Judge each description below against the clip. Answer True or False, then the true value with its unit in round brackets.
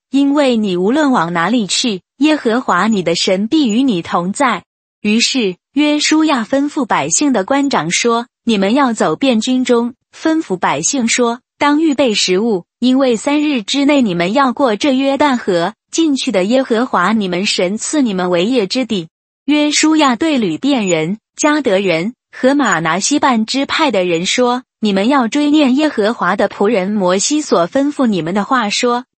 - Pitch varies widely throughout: True (5.9 semitones)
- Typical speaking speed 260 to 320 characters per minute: False (250 characters per minute)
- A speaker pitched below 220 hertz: False (245 Hz)